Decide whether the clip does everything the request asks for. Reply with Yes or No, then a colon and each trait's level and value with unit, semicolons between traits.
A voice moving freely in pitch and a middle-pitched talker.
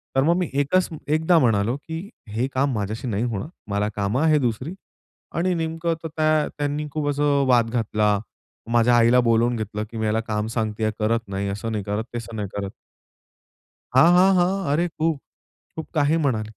No: wide, 6.4 semitones; low, 125 Hz